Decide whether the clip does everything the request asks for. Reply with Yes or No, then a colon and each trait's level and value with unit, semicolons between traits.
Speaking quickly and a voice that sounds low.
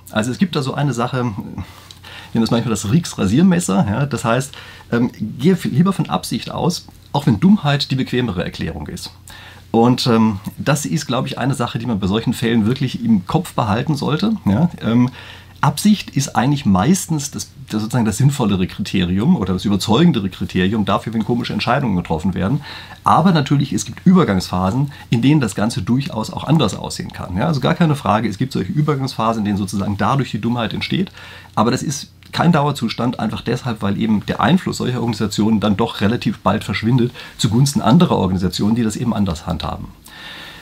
No: average, 180 wpm; low, 120 Hz